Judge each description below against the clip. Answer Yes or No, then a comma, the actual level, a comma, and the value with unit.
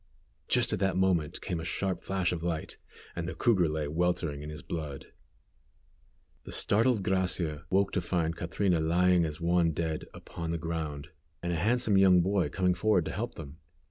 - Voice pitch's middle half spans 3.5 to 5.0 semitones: No, average, 2.9 semitones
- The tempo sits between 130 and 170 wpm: No, average, 180 wpm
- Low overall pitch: Yes, very low, 85 Hz